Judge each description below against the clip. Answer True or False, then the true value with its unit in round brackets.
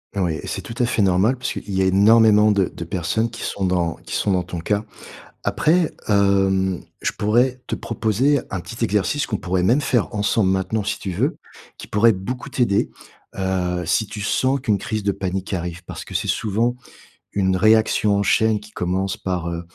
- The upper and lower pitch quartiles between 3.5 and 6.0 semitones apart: False (3.1 semitones)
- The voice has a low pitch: True (100 Hz)